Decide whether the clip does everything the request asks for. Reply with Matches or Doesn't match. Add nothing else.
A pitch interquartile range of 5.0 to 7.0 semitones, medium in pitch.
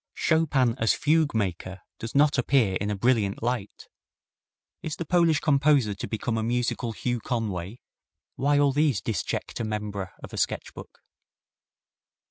Doesn't match